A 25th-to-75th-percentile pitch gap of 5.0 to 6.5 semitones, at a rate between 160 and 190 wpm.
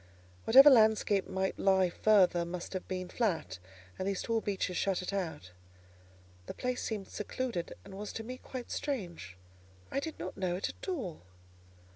No: average, 4.0 semitones; average, 165 wpm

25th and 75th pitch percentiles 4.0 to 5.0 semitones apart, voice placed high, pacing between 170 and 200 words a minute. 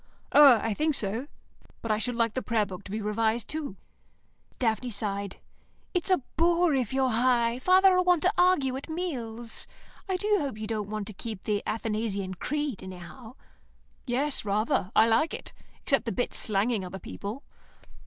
No: wide, 5.4 semitones; high, 230 Hz; average, 175 wpm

